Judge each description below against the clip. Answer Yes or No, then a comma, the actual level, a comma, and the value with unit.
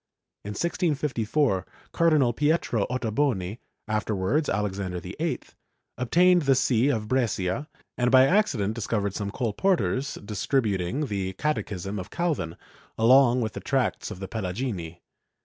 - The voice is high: No, low, 115 Hz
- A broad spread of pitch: Yes, wide, 5.7 semitones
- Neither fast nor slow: No, slow, 125 wpm